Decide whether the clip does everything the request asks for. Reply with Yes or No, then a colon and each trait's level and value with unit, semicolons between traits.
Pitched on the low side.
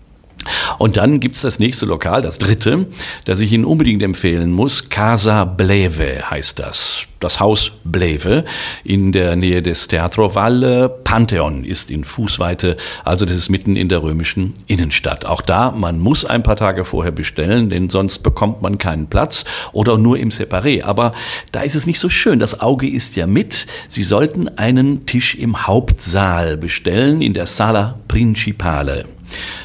Yes: low, 100 Hz